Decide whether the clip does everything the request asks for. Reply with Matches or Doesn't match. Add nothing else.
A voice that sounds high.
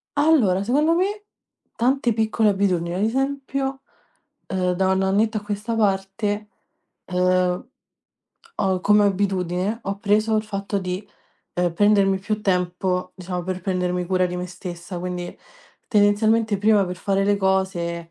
Matches